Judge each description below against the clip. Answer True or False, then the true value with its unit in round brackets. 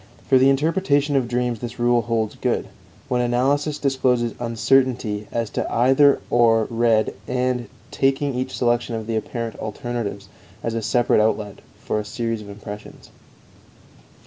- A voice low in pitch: True (120 Hz)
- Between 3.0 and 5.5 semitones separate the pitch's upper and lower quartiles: False (2.5 semitones)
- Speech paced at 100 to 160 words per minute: True (145 wpm)